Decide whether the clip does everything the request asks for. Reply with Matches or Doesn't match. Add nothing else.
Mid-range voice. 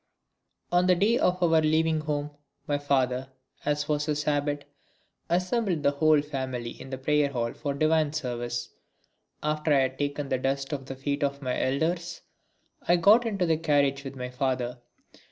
Matches